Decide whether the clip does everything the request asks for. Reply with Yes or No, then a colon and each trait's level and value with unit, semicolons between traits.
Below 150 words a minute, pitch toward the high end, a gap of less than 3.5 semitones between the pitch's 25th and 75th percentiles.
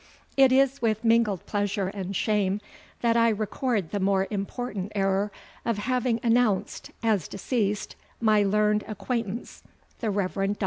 Yes: average, 140 wpm; high, 210 Hz; average, 2.8 semitones